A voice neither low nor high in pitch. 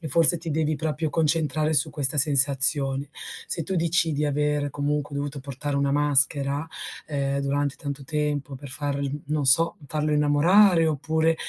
Yes: medium, 145 Hz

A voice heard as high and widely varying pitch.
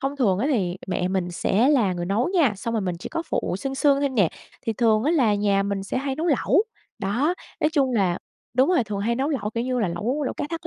Yes: high, 235 Hz; wide, 5.9 semitones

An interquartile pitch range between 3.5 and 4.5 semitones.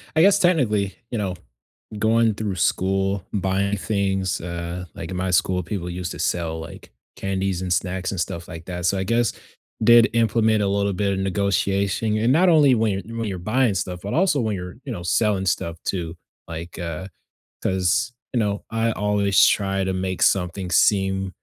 No: average, 3.1 semitones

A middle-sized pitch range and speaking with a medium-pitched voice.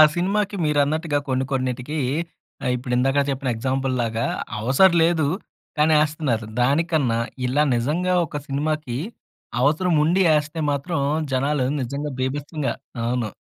Yes: average, 3.5 semitones; medium, 145 Hz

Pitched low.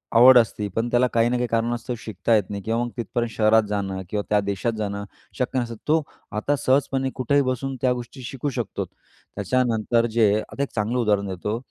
Yes: low, 115 Hz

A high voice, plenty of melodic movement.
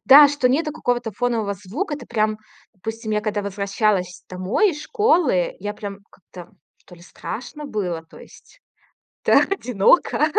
Yes: high, 215 Hz; wide, 6.1 semitones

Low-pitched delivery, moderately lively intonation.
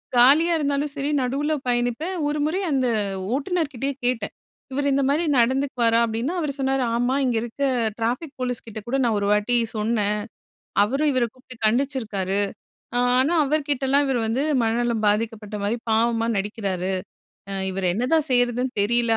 No: high, 245 Hz; average, 3.7 semitones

